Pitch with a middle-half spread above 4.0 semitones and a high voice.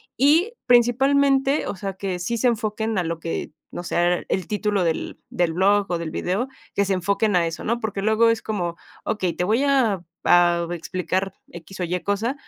Yes: average, 4.5 semitones; high, 200 Hz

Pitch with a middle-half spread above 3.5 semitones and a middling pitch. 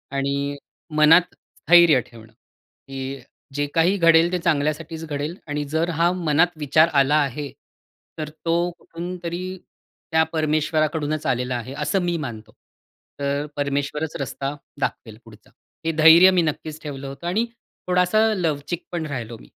No: average, 3.2 semitones; medium, 155 Hz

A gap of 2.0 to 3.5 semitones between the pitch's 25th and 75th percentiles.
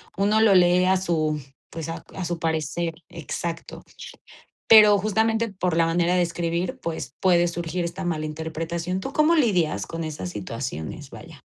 Yes: narrow, 2.5 semitones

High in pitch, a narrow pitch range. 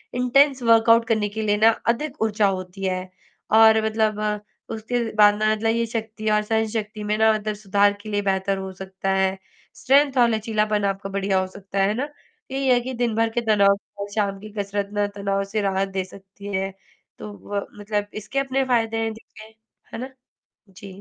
Yes: high, 215 Hz; narrow, 2.1 semitones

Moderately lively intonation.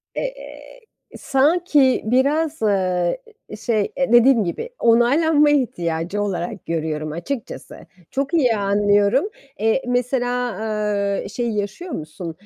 No: wide, 5.8 semitones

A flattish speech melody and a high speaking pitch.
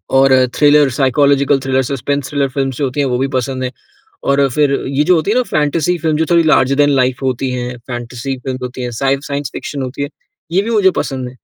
No: narrow, 2.3 semitones; low, 135 Hz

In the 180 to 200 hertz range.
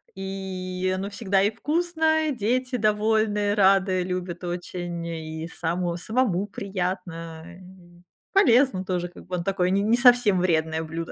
Yes: high, 190 Hz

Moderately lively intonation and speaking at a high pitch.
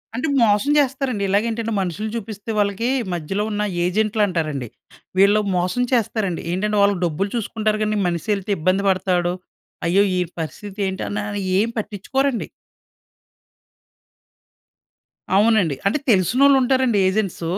Yes: average, 3.2 semitones; high, 205 Hz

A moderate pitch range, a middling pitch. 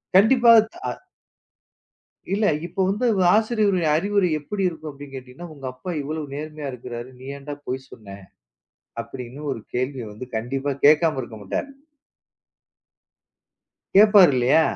No: wide, 6.9 semitones; medium, 150 Hz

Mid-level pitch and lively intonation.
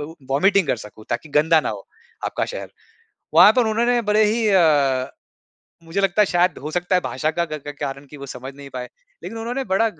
Yes: medium, 165 Hz; wide, 6.8 semitones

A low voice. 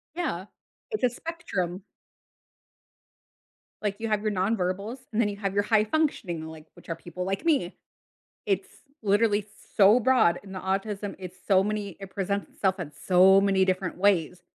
No: high, 195 Hz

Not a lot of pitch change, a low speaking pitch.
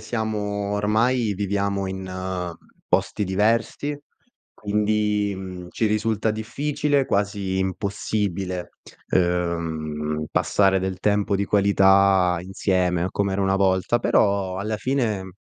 Yes: narrow, 2.2 semitones; low, 100 Hz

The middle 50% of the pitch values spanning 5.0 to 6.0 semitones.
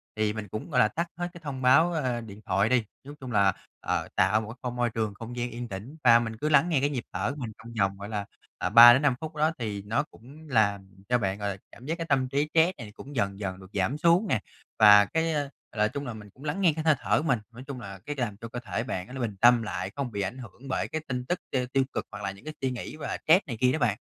Yes: average, 5.3 semitones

